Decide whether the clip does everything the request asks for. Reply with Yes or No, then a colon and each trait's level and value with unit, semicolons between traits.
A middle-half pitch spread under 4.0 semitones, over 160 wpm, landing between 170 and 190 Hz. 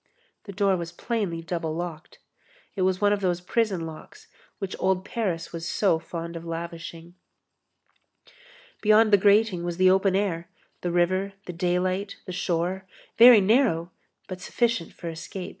No: average, 2.9 semitones; average, 155 wpm; medium, 185 Hz